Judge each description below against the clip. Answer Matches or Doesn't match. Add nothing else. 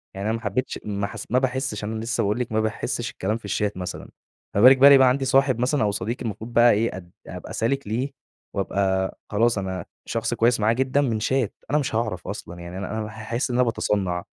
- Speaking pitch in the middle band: Doesn't match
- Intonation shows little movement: Doesn't match